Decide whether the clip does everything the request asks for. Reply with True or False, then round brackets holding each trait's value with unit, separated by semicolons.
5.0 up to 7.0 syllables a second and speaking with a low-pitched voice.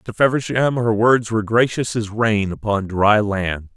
False (4.4 syllables/s; 110 Hz)